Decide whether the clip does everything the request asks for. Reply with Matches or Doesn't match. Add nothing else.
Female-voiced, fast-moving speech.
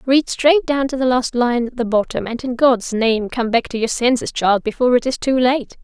Matches